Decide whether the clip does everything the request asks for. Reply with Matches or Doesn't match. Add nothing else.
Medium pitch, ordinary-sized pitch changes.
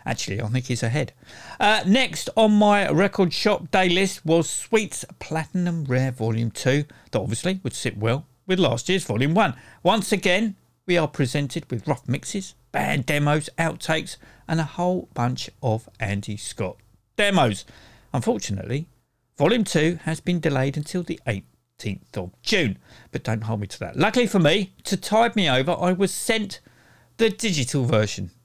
Doesn't match